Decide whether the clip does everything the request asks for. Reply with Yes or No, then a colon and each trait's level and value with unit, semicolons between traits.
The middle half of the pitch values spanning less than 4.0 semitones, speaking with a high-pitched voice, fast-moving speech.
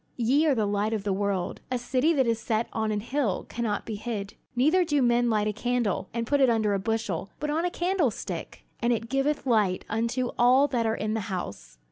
Yes: average, 3.6 semitones; high, 230 Hz; fast, 225 wpm